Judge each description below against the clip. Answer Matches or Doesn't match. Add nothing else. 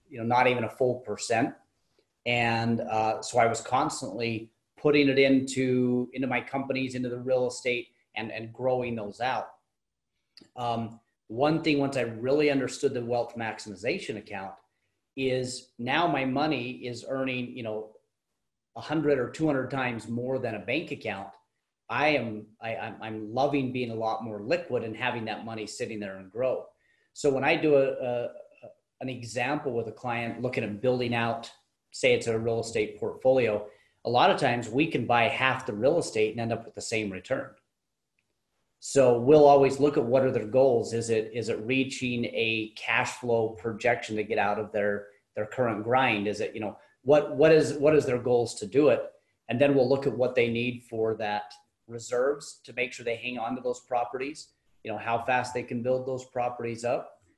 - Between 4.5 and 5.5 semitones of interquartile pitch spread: Doesn't match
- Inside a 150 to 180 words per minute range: Doesn't match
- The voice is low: Matches